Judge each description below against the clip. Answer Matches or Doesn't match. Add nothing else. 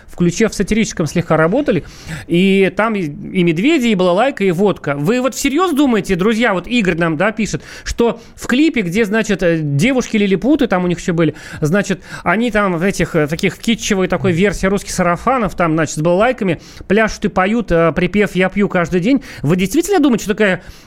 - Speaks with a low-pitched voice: Doesn't match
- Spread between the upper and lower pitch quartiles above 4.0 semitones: Matches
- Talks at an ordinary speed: Doesn't match